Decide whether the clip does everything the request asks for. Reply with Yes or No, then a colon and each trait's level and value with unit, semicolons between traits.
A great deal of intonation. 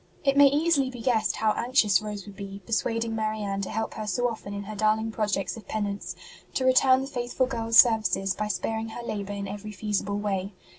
No: average, 2.8 semitones